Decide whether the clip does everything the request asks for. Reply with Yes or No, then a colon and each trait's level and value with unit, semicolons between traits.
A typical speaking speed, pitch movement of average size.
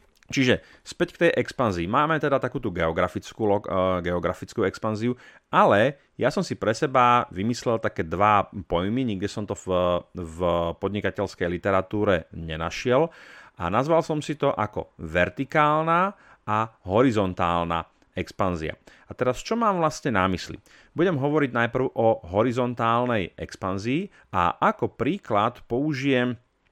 No: average, 125 wpm; wide, 6.2 semitones